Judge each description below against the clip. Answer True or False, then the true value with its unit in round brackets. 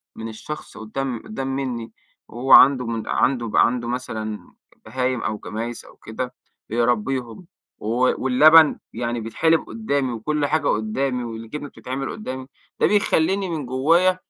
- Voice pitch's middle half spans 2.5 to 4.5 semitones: True (3.9 semitones)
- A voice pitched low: True (130 Hz)